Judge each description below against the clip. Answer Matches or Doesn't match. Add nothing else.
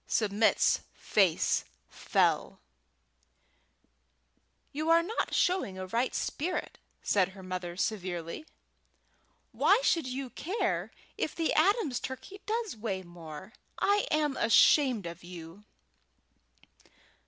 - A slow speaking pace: Matches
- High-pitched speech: Matches